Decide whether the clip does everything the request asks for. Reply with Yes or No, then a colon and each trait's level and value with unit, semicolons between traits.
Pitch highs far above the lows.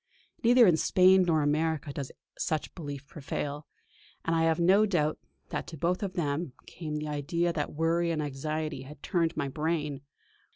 No: narrow, 2.6 semitones